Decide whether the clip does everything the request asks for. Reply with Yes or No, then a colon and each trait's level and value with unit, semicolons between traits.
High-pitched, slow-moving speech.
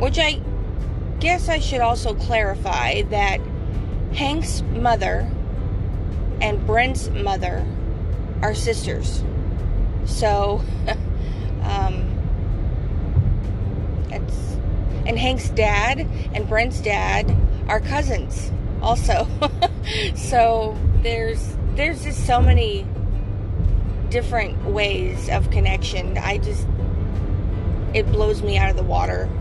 No: very low, 95 Hz; slow, 95 wpm